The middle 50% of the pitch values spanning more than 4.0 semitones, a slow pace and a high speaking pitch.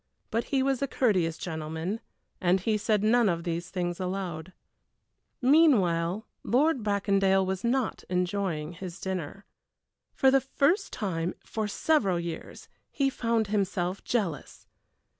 Yes: average, 5.1 semitones; slow, 130 wpm; high, 195 Hz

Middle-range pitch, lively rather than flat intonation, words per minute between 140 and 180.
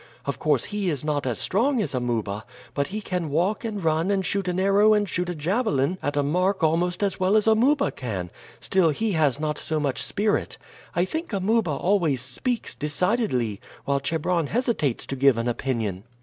No: medium, 175 Hz; wide, 6.5 semitones; average, 190 wpm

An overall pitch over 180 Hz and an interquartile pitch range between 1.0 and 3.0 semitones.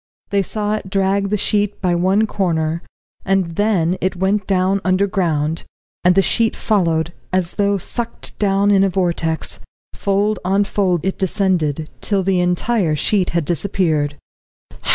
Yes: high, 190 Hz; narrow, 2.6 semitones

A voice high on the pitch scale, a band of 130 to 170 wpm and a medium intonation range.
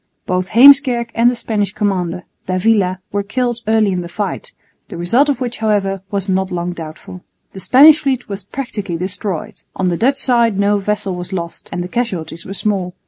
No: high, 200 Hz; average, 190 wpm; average, 4.5 semitones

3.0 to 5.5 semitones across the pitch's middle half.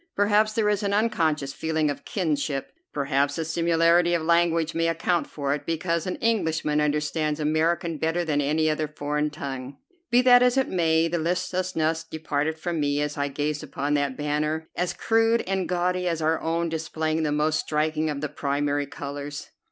No: narrow, 2.5 semitones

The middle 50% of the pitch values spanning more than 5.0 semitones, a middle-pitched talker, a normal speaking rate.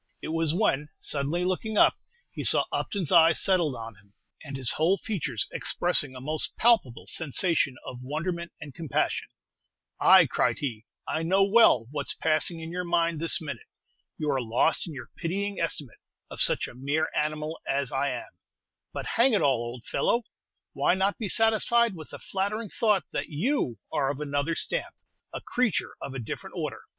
Yes: wide, 5.4 semitones; medium, 160 Hz; average, 180 wpm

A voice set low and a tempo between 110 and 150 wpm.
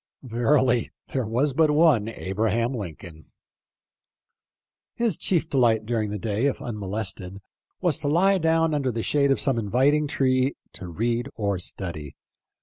Yes: low, 120 Hz; average, 145 wpm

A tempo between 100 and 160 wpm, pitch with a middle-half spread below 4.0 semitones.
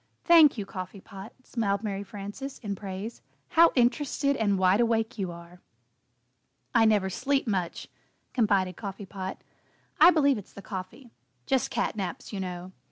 No: average, 155 wpm; average, 4.4 semitones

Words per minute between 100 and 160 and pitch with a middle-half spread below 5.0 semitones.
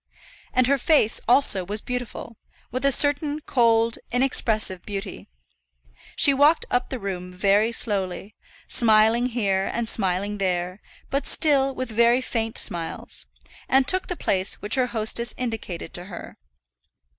Yes: average, 140 wpm; average, 4.5 semitones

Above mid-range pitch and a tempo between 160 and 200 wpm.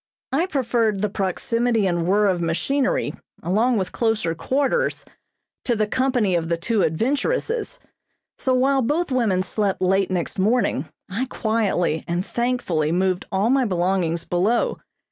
No: high, 210 Hz; average, 145 wpm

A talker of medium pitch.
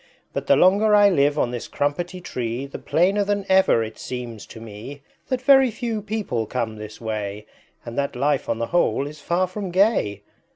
Yes: medium, 145 Hz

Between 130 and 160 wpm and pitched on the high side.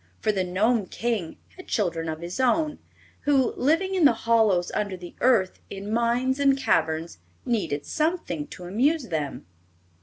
Yes: average, 155 wpm; high, 220 Hz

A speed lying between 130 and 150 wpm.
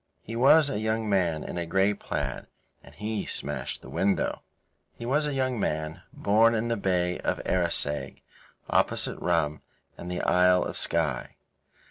No: average, 160 wpm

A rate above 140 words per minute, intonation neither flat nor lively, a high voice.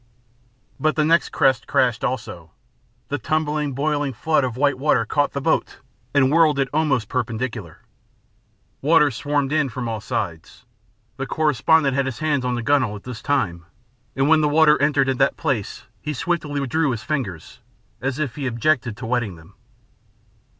No: average, 170 wpm; average, 4.0 semitones; low, 135 Hz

